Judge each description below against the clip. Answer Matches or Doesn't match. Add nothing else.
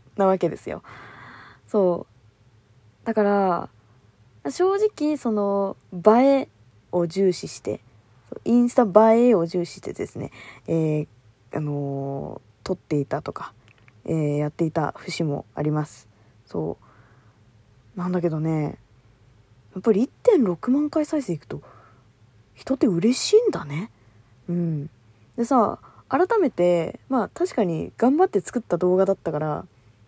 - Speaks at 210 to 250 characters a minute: Matches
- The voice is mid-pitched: Matches